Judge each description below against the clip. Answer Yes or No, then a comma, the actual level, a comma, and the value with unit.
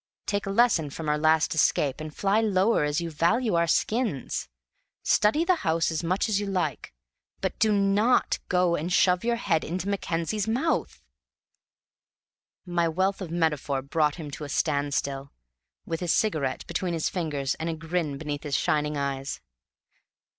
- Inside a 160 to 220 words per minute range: Yes, average, 170 wpm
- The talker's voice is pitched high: No, medium, 170 Hz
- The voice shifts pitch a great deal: No, average, 4.7 semitones